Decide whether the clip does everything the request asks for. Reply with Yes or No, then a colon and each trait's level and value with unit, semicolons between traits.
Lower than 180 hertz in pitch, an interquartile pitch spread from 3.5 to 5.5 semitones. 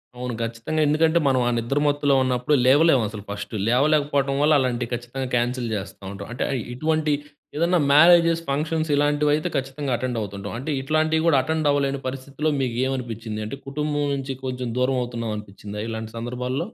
Yes: low, 135 Hz; average, 3.8 semitones